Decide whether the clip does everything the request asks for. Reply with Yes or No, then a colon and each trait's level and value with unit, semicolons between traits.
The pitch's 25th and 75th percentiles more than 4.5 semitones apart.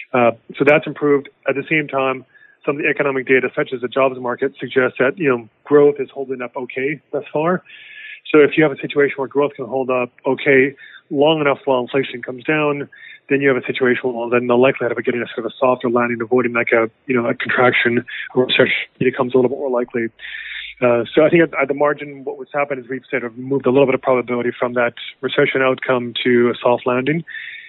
No: narrow, 2.5 semitones